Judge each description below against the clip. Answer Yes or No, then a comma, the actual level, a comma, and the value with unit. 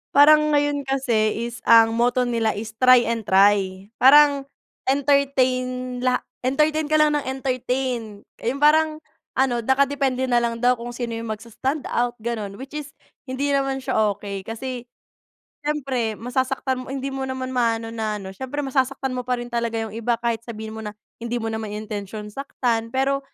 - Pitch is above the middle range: Yes, very high, 250 Hz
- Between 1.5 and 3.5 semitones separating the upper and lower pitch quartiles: Yes, average, 3.0 semitones